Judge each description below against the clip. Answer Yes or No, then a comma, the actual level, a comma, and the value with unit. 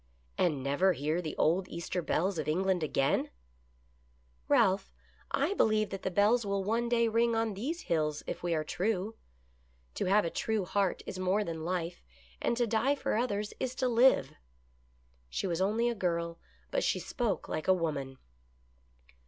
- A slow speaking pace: No, average, 180 wpm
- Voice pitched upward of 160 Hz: Yes, high, 190 Hz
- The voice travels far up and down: No, average, 5.0 semitones